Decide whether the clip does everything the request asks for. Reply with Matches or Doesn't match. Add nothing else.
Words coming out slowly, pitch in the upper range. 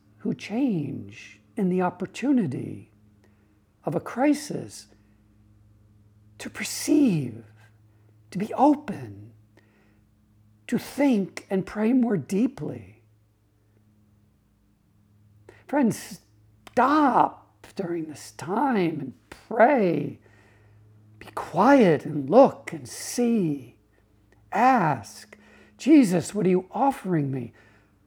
Doesn't match